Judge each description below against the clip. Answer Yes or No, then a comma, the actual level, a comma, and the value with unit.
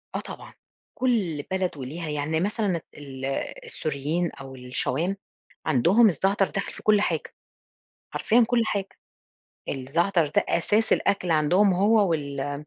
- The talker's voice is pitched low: No, medium, 170 Hz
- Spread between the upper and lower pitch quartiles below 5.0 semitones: No, wide, 5.6 semitones